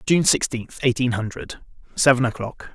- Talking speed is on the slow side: Yes, slow, 130 wpm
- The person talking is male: Yes, male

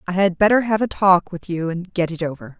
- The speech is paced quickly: Yes, fast, 280 wpm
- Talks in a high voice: No, medium, 180 Hz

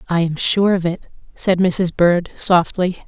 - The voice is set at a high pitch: No, medium, 180 Hz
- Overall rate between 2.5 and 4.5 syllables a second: Yes, 4.1 syllables/s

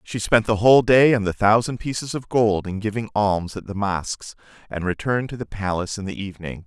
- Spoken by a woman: No, male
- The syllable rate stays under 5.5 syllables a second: No, 5.7 syllables/s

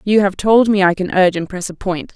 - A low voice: No, high, 190 Hz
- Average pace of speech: No, fast, 305 wpm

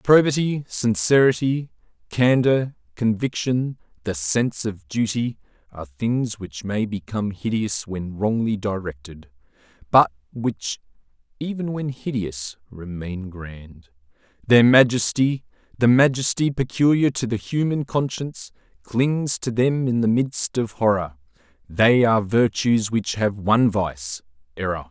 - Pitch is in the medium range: No, low, 110 Hz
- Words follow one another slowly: Yes, slow, 115 wpm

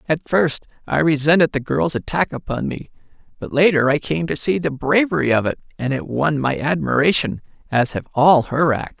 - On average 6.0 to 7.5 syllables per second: No, 5.2 syllables/s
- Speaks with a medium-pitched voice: Yes, medium, 145 Hz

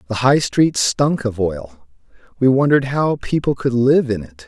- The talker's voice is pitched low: Yes, low, 125 Hz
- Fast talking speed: No, average, 190 wpm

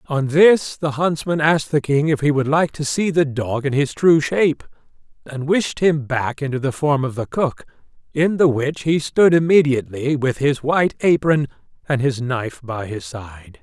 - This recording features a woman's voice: No, male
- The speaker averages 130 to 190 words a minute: No, average, 200 wpm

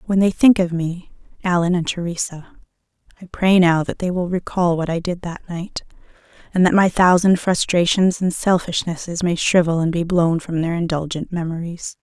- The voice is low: No, medium, 175 Hz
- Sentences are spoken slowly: No, average, 180 wpm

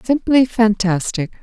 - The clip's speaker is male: No, female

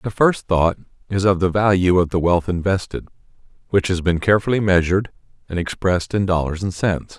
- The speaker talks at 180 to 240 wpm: Yes, average, 185 wpm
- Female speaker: No, male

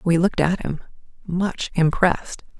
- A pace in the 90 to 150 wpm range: Yes, average, 140 wpm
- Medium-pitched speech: Yes, medium, 175 Hz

